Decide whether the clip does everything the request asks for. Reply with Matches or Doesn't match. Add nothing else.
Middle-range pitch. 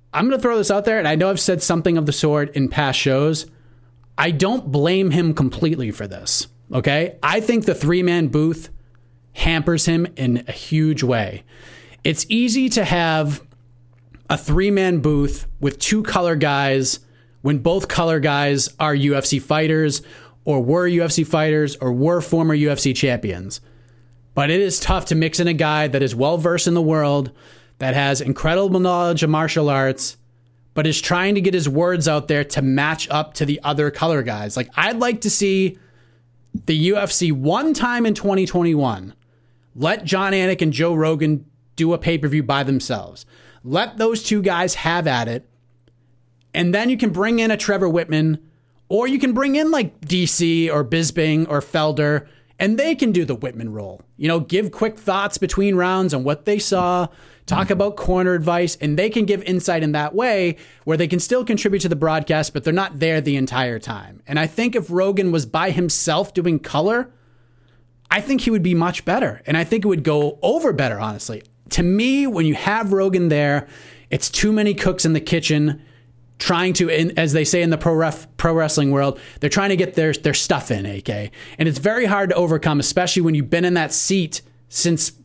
Matches